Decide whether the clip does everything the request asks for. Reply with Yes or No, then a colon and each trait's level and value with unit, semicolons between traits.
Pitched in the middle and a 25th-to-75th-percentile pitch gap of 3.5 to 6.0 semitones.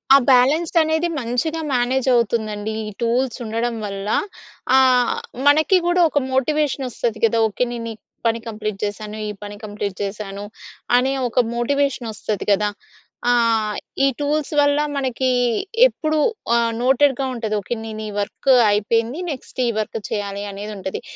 No: high, 235 Hz; average, 4.2 semitones